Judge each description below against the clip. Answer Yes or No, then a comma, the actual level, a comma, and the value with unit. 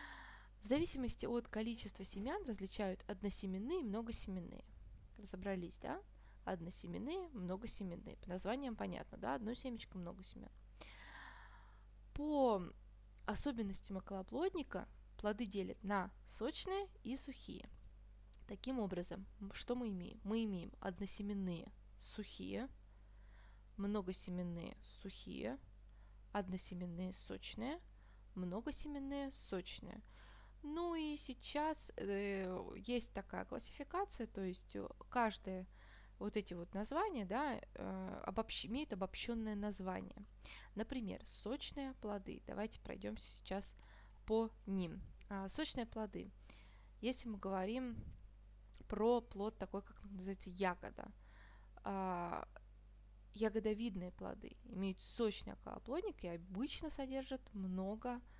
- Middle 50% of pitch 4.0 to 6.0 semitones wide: Yes, average, 4.4 semitones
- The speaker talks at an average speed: No, slow, 95 wpm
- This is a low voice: No, high, 200 Hz